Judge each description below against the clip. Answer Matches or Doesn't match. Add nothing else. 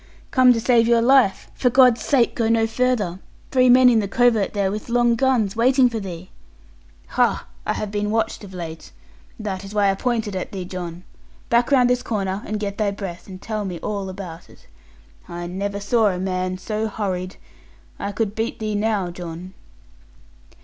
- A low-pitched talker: Doesn't match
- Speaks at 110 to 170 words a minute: Doesn't match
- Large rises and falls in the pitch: Doesn't match